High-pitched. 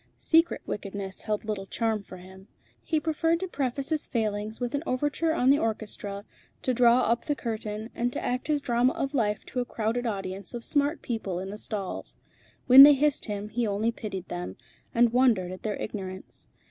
Yes: high, 230 Hz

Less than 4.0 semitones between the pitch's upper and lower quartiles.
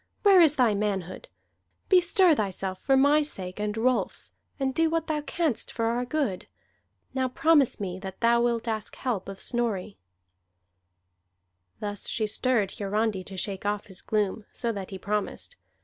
No: average, 5.2 semitones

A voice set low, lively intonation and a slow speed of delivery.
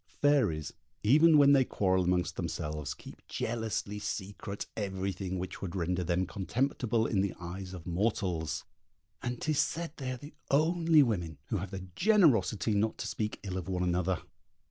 No: low, 100 Hz; wide, 5.8 semitones; average, 165 wpm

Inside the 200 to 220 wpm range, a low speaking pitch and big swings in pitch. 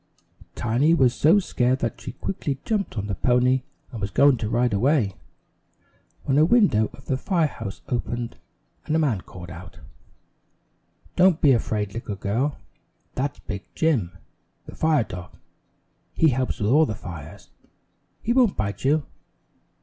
No: average, 155 wpm; low, 125 Hz; wide, 6.4 semitones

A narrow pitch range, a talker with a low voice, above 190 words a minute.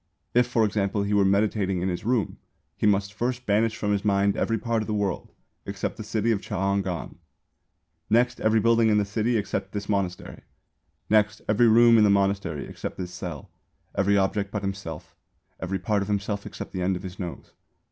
Yes: narrow, 1.9 semitones; low, 100 Hz; average, 200 wpm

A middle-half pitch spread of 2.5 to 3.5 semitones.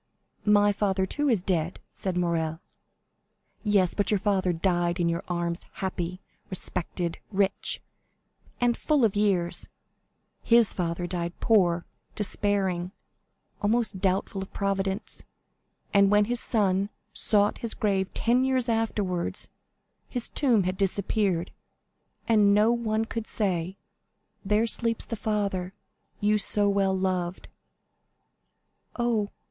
Yes: average, 2.8 semitones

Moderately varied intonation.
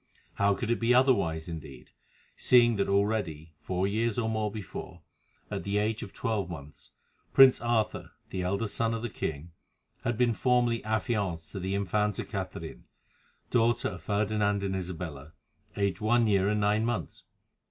Yes: average, 3.7 semitones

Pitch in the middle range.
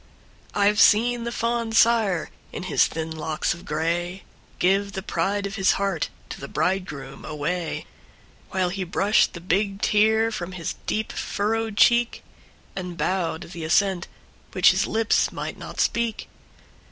No: high, 195 Hz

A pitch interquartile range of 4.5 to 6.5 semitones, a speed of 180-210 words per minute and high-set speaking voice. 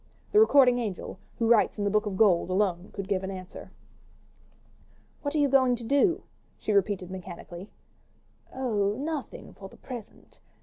No: average, 5.2 semitones; average, 165 wpm; high, 210 Hz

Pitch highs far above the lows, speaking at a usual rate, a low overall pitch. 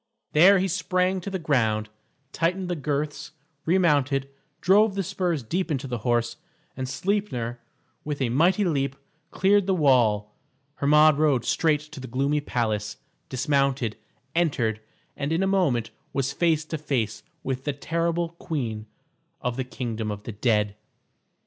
No: wide, 5.9 semitones; average, 150 wpm; medium, 145 Hz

